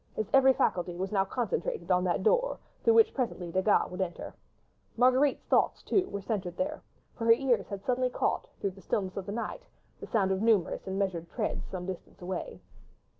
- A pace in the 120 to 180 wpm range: No, average, 195 wpm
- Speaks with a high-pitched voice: Yes, high, 200 Hz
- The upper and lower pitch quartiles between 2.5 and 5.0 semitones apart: No, wide, 5.4 semitones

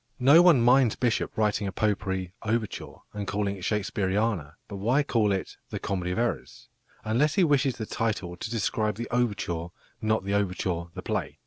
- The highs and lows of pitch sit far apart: No, average, 3.5 semitones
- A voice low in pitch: Yes, low, 105 Hz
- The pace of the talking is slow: No, average, 180 wpm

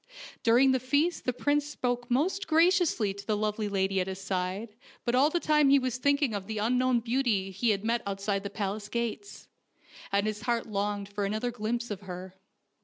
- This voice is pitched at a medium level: No, high, 225 Hz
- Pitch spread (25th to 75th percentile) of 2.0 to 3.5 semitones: No, average, 4.3 semitones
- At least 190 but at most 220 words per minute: Yes, average, 200 wpm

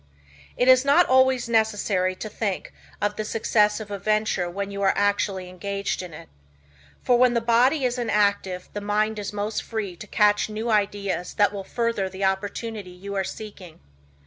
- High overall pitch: Yes, high, 210 Hz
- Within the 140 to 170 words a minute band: No, average, 180 wpm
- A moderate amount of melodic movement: No, narrow, 2.3 semitones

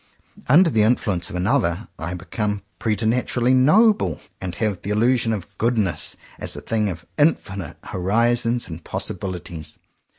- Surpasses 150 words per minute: No, average, 140 wpm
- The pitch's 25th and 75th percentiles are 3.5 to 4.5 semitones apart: No, average, 5.0 semitones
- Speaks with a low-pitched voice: Yes, low, 105 Hz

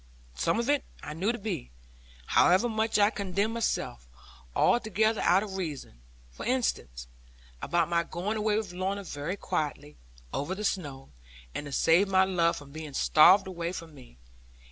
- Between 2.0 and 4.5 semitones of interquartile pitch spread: No, wide, 5.5 semitones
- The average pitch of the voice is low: No, medium, 185 Hz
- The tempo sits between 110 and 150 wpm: No, average, 165 wpm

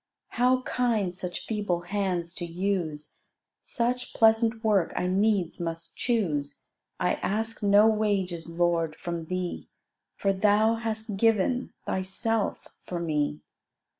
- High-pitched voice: Yes, high, 195 Hz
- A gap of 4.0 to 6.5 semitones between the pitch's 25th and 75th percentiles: Yes, average, 4.3 semitones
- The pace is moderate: No, slow, 120 wpm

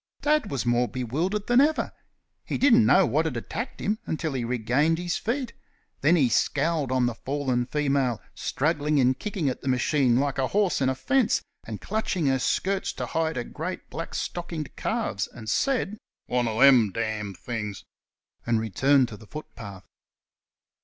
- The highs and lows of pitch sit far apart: Yes, wide, 6.4 semitones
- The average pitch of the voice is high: No, medium, 140 Hz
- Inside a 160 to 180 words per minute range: Yes, average, 175 wpm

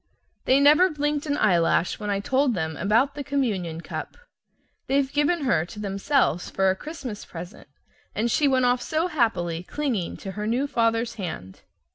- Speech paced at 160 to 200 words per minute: Yes, average, 170 wpm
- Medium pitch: No, high, 235 Hz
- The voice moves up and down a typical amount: No, wide, 6.8 semitones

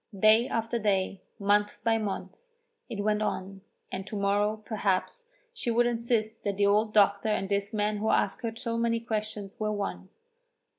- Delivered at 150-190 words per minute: Yes, average, 170 wpm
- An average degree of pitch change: No, narrow, 2.1 semitones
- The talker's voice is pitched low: No, high, 215 Hz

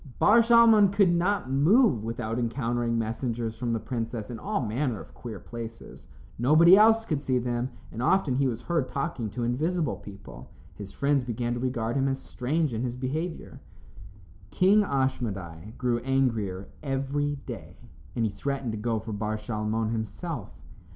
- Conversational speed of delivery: Yes, average, 165 wpm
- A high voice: No, low, 125 Hz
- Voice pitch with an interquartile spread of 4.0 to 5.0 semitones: Yes, average, 4.4 semitones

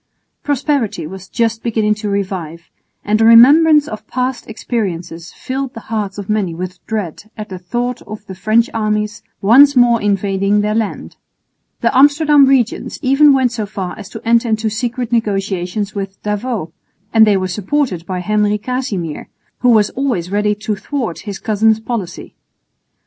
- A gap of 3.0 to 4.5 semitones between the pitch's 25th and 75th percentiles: Yes, average, 3.6 semitones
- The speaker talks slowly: No, average, 160 wpm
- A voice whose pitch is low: No, high, 215 Hz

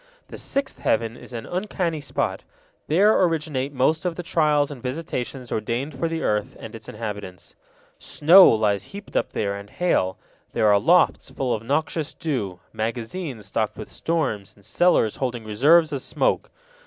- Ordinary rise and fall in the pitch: No, wide, 7.0 semitones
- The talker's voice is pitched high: No, low, 130 Hz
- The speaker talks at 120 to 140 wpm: No, average, 165 wpm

